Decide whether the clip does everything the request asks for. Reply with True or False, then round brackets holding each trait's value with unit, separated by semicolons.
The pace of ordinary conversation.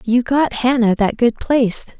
True (180 wpm)